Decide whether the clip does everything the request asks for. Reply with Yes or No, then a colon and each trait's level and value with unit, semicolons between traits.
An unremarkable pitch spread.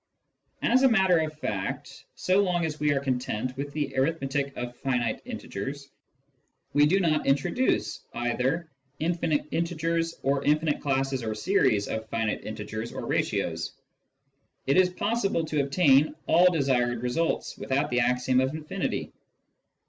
Yes: average, 4.7 semitones